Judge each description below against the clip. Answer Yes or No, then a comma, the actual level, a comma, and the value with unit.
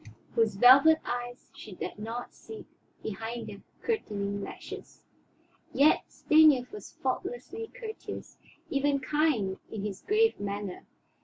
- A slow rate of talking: Yes, slow, 120 wpm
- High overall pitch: Yes, high, 245 Hz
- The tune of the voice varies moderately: No, wide, 7.2 semitones